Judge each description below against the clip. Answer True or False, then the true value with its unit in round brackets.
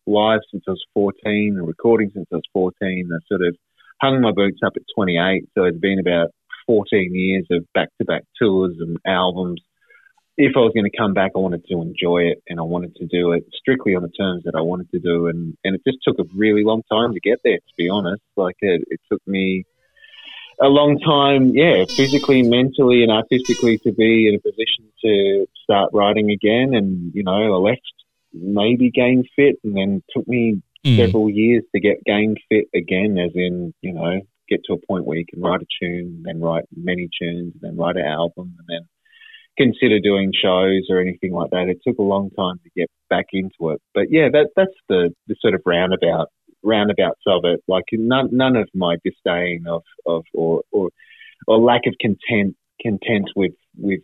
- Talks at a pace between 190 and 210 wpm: True (205 wpm)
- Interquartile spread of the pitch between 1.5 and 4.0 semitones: False (4.7 semitones)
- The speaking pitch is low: True (100 Hz)